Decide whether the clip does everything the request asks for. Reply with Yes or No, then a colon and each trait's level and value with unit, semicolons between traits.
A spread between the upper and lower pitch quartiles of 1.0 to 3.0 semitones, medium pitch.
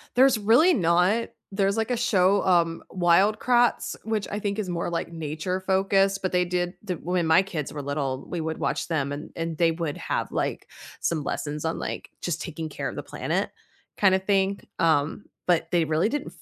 No: average, 3.6 semitones; medium, 180 Hz